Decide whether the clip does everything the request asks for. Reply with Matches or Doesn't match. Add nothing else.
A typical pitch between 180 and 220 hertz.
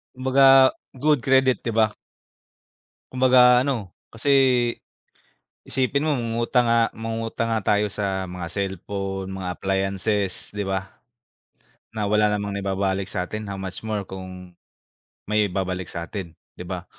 Doesn't match